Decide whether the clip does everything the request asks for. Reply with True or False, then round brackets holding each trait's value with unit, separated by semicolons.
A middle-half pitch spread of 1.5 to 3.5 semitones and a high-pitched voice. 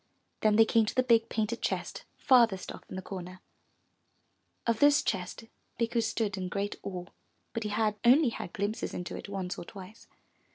True (3.2 semitones; 215 Hz)